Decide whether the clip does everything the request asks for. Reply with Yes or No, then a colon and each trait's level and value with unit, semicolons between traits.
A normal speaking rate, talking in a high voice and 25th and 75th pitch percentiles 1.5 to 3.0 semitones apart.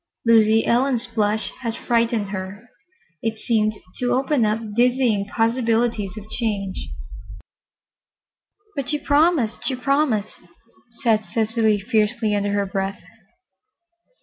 No: slow, 105 wpm; high, 225 Hz; narrow, 2.5 semitones